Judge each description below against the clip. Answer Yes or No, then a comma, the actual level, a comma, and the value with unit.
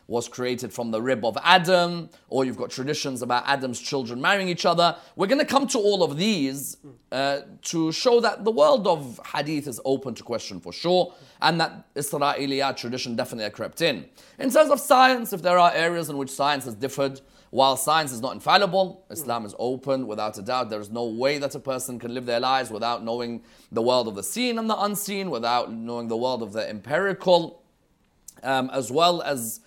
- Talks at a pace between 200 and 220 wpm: Yes, fast, 205 wpm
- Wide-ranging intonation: Yes, wide, 6.4 semitones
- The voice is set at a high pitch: No, medium, 140 Hz